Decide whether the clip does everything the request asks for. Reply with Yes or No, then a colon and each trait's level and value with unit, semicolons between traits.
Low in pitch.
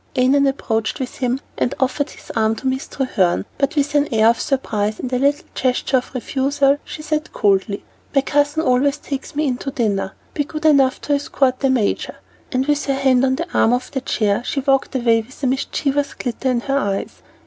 No: very high, 265 Hz